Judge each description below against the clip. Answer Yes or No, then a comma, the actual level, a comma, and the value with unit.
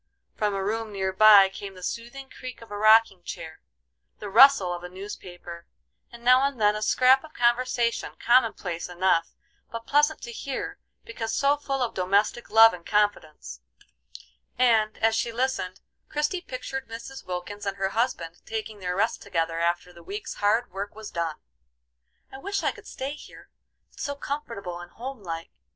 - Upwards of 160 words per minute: Yes, average, 175 wpm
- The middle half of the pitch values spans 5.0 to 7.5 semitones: Yes, average, 5.3 semitones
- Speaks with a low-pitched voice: No, high, 215 Hz